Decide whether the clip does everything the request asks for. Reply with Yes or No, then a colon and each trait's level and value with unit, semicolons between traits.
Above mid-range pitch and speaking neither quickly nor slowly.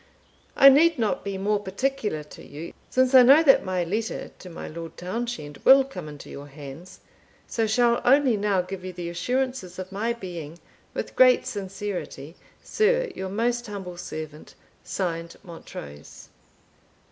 Yes: high, 195 Hz; average, 155 wpm